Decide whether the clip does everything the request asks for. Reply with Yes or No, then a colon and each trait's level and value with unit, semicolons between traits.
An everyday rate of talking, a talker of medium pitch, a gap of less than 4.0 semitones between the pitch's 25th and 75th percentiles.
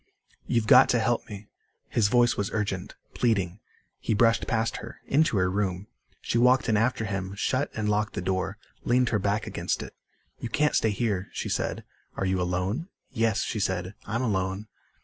No: average, 185 wpm; low, 105 Hz; average, 3.5 semitones